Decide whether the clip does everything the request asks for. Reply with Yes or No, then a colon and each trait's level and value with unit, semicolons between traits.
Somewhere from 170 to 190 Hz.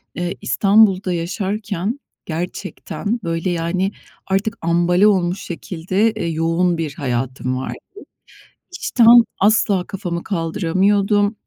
Yes: medium, 185 Hz